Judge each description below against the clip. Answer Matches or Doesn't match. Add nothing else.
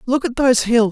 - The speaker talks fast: Matches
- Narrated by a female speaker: Matches